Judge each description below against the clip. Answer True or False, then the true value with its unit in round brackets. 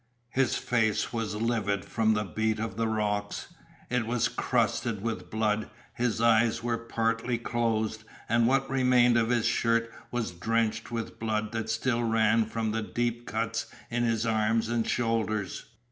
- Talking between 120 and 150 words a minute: False (160 wpm)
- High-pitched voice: False (115 Hz)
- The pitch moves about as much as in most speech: False (1.3 semitones)